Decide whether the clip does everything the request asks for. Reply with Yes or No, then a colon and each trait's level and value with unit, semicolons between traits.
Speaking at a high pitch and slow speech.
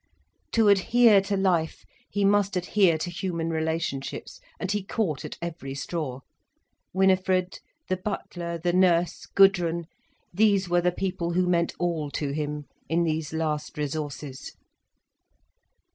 No: medium, 175 Hz; slow, 130 wpm